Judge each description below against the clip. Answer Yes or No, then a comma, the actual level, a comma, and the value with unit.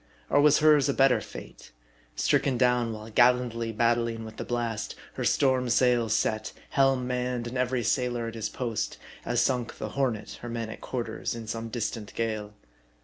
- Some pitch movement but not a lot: No, narrow, 1.9 semitones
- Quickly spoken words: No, average, 175 wpm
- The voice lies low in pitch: Yes, low, 120 Hz